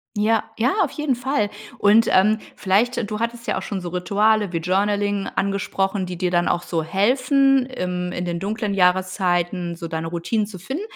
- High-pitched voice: Yes, high, 200 Hz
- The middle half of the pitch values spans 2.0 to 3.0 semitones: No, average, 3.7 semitones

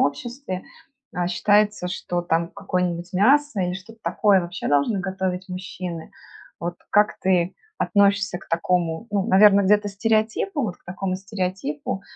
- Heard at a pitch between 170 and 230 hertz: Yes, high, 190 Hz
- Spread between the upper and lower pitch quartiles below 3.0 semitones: Yes, narrow, 2.6 semitones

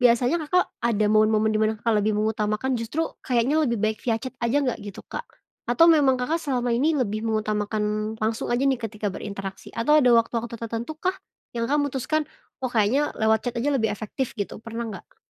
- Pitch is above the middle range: Yes, high, 230 Hz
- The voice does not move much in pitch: No, average, 3.5 semitones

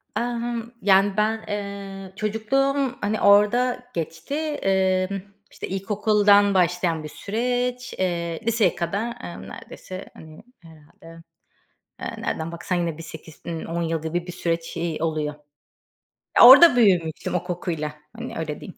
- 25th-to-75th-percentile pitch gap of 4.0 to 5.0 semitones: Yes, average, 4.7 semitones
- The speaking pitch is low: No, high, 190 Hz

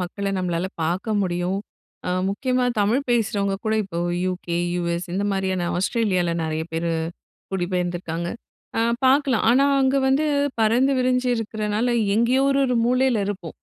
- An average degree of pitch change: No, wide, 5.8 semitones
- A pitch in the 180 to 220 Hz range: Yes, high, 200 Hz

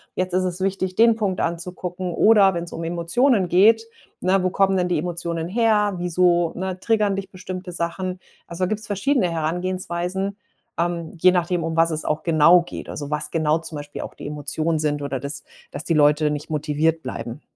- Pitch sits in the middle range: Yes, medium, 175 Hz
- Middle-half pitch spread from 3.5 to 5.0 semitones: No, average, 2.7 semitones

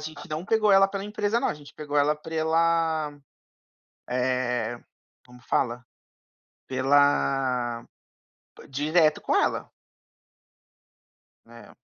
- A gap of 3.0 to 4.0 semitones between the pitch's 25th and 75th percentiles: No, average, 4.4 semitones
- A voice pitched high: No, medium, 150 Hz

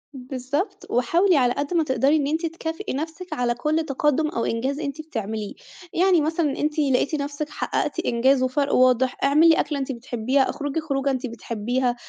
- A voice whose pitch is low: No, very high, 280 Hz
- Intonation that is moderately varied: Yes, average, 3.5 semitones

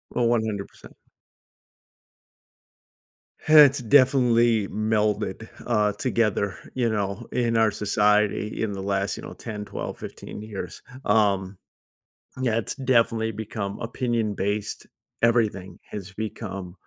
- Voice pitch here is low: Yes, low, 110 Hz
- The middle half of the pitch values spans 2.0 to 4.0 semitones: Yes, narrow, 2.4 semitones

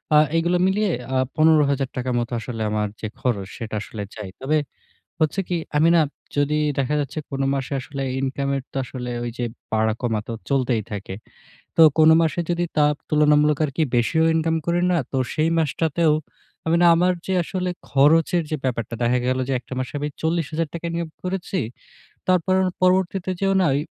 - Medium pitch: Yes, medium, 150 Hz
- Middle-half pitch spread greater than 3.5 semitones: Yes, average, 4.8 semitones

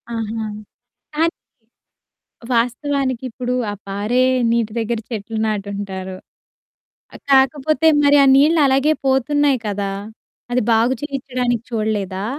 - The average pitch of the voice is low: No, high, 245 Hz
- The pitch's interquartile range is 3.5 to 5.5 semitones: Yes, average, 4.1 semitones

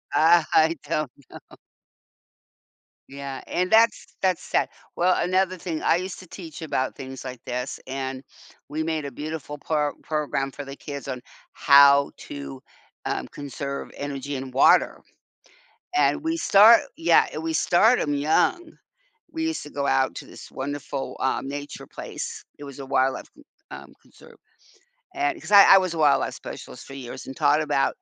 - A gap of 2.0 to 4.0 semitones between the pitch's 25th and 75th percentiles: No, average, 4.9 semitones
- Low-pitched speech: No, medium, 145 Hz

